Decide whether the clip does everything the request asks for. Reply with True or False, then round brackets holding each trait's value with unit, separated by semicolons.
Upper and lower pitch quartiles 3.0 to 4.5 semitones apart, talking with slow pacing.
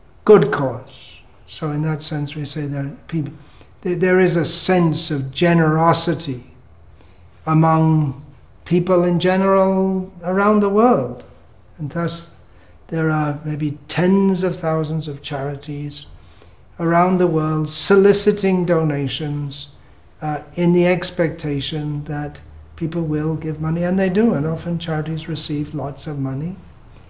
True (3.5 semitones; 125 wpm)